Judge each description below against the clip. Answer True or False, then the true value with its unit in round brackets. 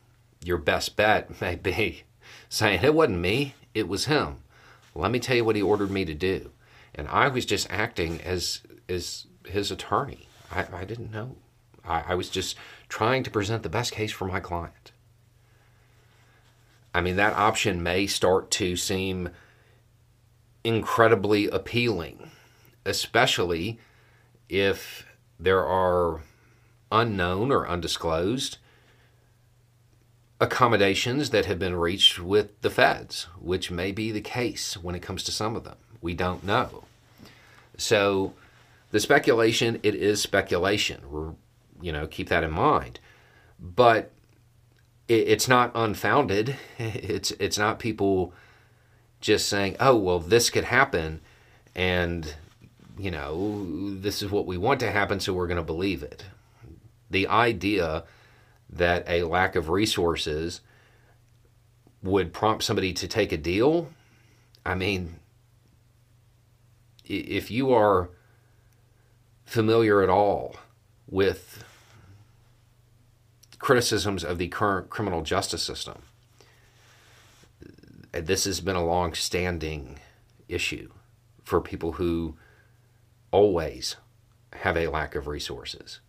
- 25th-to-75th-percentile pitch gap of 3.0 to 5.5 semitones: True (3.9 semitones)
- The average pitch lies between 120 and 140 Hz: False (110 Hz)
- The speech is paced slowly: True (125 wpm)